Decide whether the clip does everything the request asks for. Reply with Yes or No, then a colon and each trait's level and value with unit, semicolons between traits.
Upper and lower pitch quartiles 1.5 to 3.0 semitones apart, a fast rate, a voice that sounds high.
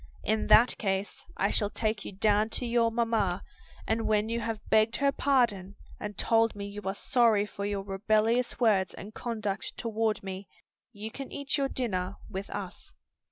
No: narrow, 2.4 semitones; average, 175 wpm; high, 215 Hz